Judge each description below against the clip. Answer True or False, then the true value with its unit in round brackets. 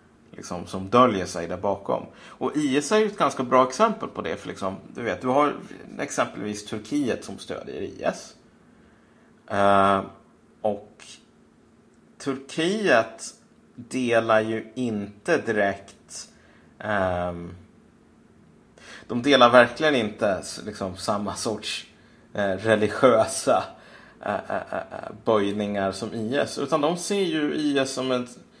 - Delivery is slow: True (120 wpm)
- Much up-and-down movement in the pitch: True (5.9 semitones)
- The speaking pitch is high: False (115 Hz)